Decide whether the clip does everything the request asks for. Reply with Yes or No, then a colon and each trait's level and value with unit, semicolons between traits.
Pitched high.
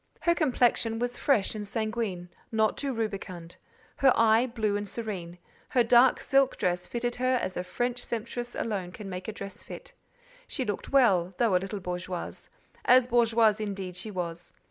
Yes: high, 220 Hz